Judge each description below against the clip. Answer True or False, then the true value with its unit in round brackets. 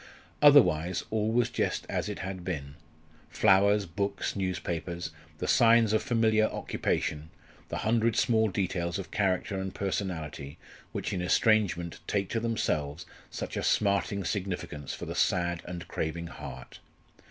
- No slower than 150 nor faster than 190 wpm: False (140 wpm)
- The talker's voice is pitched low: True (95 Hz)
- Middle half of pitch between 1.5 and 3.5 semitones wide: False (3.9 semitones)